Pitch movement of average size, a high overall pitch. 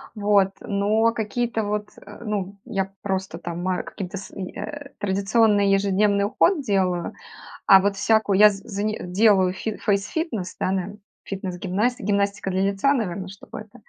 No: narrow, 1.9 semitones; high, 200 Hz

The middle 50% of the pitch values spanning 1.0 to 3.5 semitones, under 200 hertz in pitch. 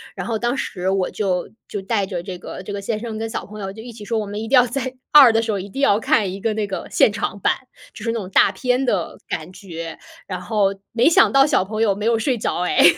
No: average, 3.1 semitones; high, 215 Hz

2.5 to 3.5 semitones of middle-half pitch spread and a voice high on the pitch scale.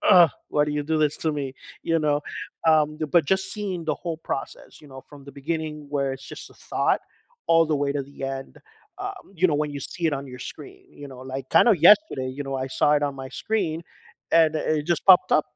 No: average, 3.2 semitones; medium, 150 Hz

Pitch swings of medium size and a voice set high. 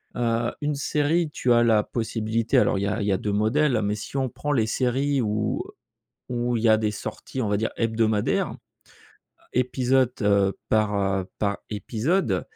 No: average, 3.4 semitones; low, 115 Hz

